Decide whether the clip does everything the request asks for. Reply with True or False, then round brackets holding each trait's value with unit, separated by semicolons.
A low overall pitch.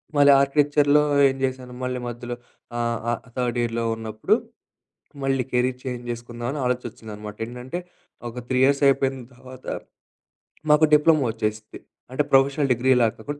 True (125 Hz)